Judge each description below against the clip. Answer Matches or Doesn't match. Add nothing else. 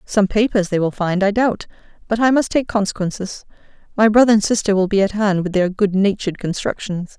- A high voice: Matches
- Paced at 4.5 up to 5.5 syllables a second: Doesn't match